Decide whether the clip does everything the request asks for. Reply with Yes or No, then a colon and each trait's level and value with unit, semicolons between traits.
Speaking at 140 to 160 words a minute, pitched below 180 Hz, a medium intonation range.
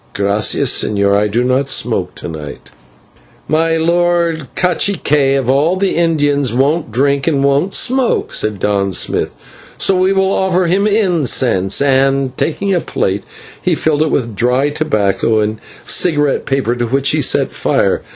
No: average, 155 wpm; medium, 140 Hz; wide, 6.4 semitones